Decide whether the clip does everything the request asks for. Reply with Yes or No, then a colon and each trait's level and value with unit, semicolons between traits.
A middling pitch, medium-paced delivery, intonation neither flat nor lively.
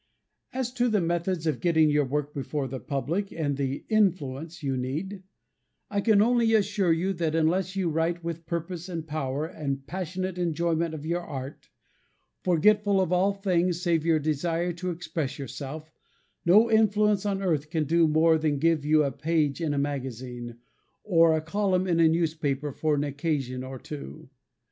Yes: medium, 165 Hz; average, 170 wpm; average, 3.8 semitones